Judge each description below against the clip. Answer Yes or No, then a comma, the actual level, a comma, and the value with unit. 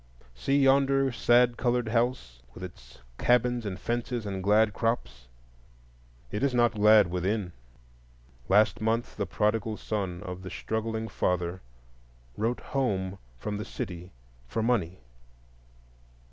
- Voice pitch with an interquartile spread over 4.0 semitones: Yes, average, 4.4 semitones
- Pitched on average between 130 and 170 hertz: No, low, 110 Hz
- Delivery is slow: Yes, slow, 125 wpm